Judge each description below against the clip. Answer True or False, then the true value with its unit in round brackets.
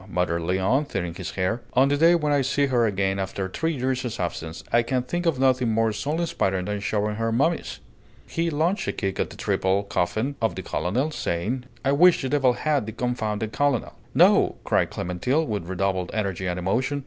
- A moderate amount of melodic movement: False (6.5 semitones)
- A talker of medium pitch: False (115 Hz)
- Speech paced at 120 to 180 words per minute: False (200 wpm)